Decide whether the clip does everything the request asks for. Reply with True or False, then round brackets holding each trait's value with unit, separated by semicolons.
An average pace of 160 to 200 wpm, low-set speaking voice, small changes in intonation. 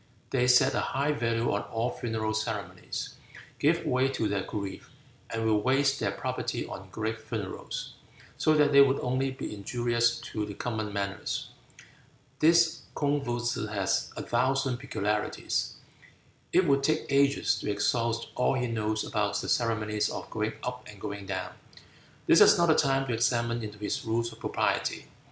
False (165 wpm; 115 Hz; 3.8 semitones)